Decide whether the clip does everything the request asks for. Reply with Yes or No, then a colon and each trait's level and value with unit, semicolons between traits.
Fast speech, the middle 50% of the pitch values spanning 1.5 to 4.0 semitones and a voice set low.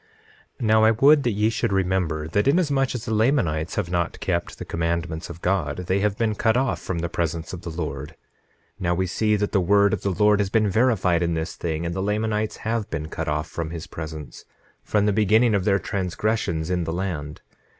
No: fast, 220 wpm; average, 4.4 semitones; very low, 95 Hz